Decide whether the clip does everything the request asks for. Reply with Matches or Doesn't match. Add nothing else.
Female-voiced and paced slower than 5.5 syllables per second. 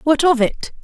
Matches